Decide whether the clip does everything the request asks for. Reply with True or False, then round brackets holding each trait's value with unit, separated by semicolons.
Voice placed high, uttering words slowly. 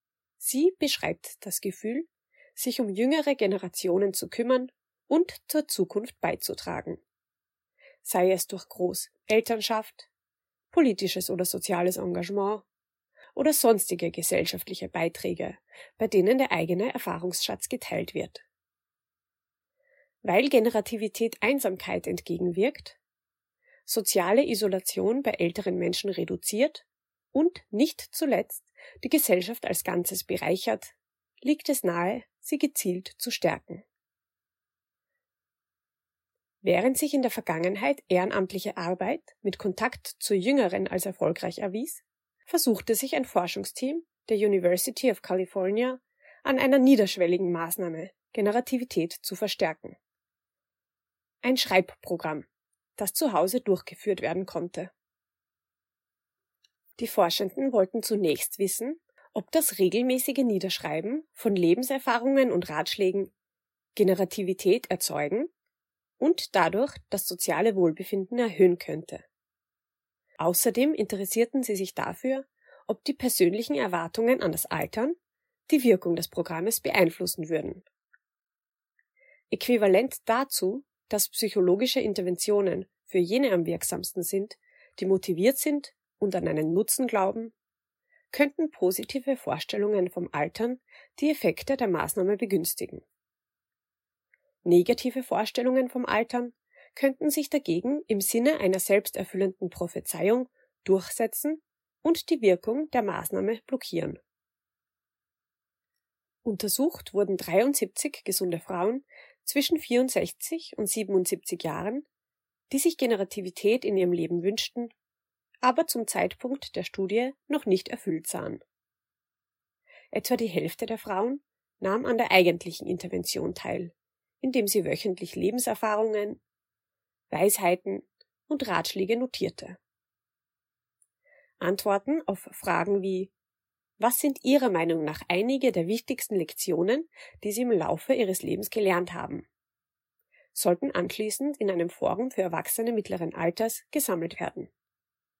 True (215 Hz; 105 wpm)